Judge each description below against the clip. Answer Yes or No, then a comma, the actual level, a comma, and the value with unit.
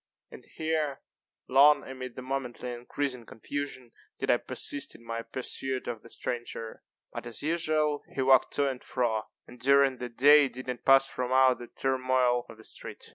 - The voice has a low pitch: Yes, low, 130 Hz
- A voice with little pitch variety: Yes, narrow, 2.2 semitones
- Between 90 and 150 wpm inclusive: No, average, 180 wpm